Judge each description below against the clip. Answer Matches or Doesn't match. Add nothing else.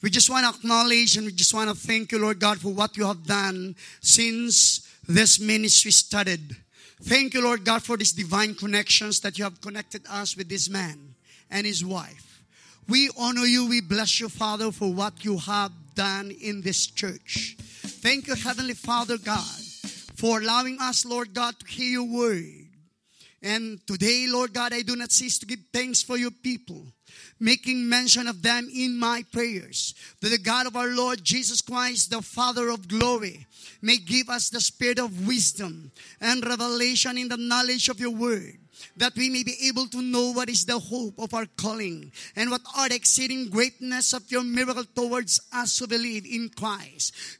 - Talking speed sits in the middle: Matches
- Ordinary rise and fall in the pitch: Matches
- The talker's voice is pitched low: Doesn't match